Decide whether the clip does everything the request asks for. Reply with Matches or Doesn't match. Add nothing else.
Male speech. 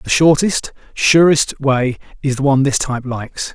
Matches